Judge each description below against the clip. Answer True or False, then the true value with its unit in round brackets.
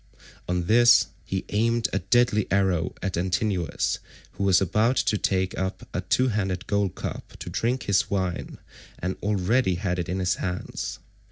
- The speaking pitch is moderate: False (95 Hz)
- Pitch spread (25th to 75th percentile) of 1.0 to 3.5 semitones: True (2.8 semitones)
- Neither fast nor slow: True (165 wpm)